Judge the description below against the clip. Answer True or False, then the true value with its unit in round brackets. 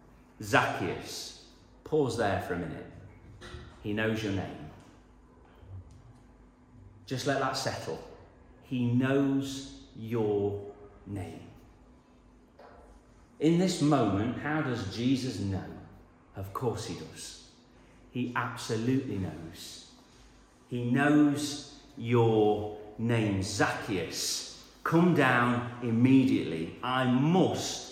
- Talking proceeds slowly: True (90 wpm)